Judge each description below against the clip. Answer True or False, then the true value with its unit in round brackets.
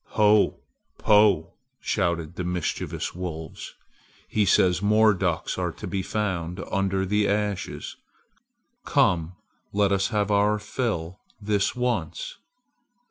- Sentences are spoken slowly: True (115 wpm)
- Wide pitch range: False (2.9 semitones)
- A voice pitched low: True (100 Hz)